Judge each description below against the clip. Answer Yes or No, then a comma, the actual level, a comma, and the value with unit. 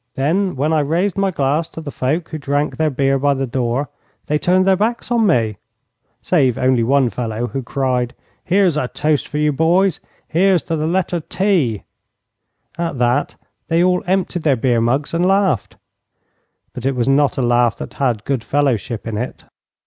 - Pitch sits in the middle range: Yes, medium, 145 Hz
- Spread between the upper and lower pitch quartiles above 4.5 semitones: Yes, average, 5.3 semitones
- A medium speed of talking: Yes, average, 185 wpm